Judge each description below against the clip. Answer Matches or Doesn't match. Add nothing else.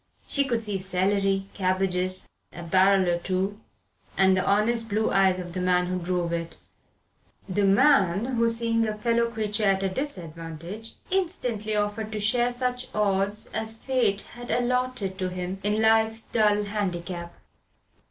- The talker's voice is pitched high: Matches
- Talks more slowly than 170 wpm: Matches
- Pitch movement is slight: Doesn't match